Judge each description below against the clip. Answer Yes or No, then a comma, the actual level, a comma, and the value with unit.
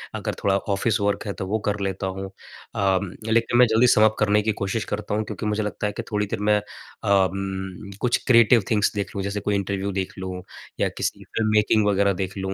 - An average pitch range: No, narrow, 1.6 semitones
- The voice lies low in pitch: Yes, low, 100 Hz